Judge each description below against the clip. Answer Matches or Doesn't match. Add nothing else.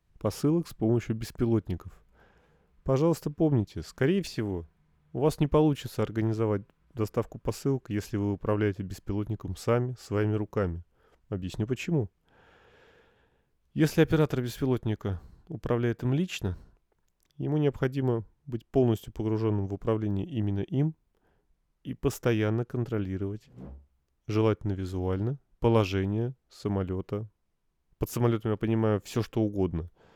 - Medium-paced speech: Doesn't match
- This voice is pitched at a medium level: Doesn't match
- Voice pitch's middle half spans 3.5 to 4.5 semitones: Matches